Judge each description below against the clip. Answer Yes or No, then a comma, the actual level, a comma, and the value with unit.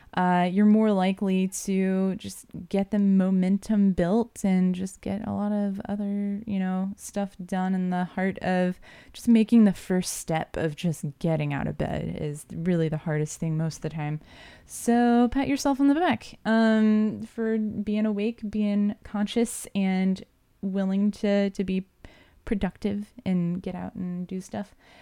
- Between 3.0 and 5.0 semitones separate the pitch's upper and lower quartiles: No, narrow, 2.5 semitones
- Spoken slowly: No, average, 165 wpm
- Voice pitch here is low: No, high, 195 Hz